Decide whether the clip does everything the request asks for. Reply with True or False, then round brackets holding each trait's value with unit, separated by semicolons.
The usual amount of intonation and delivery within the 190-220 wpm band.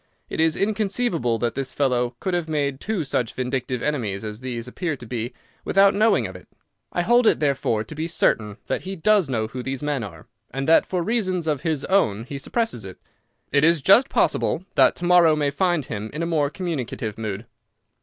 False (6.6 semitones; 205 wpm)